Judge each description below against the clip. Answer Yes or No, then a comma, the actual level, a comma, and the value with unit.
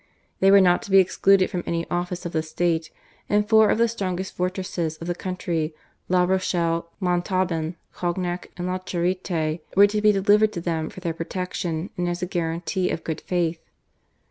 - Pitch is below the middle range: No, medium, 180 Hz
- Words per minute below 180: No, average, 185 wpm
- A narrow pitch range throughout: Yes, narrow, 2.1 semitones